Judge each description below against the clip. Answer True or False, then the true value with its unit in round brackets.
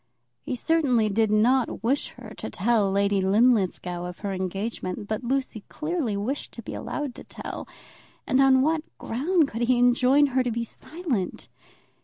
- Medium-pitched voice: False (235 Hz)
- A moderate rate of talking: True (165 wpm)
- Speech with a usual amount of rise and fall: True (4.8 semitones)